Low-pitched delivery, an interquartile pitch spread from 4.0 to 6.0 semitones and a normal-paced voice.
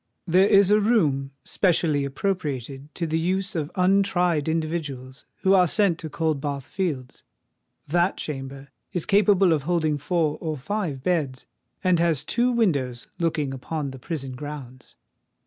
No: medium, 160 Hz; average, 4.8 semitones; average, 145 wpm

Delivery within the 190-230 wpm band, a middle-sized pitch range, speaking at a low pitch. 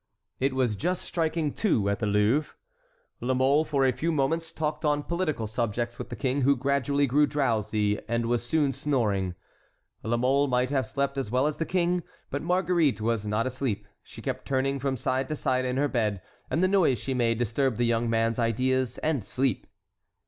Yes: average, 195 wpm; average, 3.9 semitones; low, 130 Hz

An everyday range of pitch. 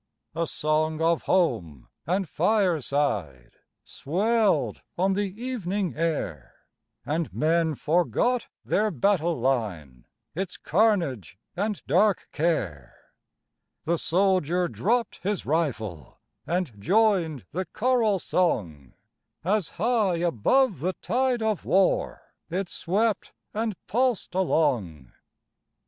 No: wide, 6.2 semitones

